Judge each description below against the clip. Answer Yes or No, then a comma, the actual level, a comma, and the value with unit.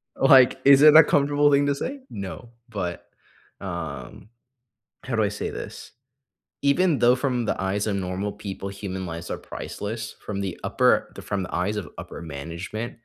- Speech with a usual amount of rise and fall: No, wide, 6.1 semitones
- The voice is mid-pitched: No, low, 105 Hz